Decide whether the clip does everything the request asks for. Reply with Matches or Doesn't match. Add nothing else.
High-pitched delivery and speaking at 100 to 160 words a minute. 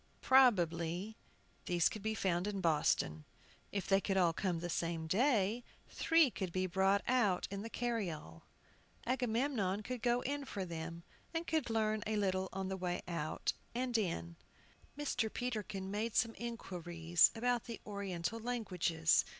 Matches